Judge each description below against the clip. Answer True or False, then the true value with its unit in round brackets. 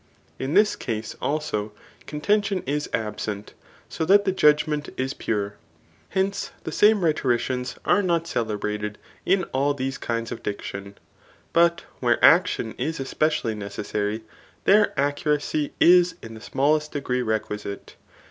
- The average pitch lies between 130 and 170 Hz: True (140 Hz)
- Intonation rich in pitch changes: True (7.1 semitones)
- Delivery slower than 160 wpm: True (135 wpm)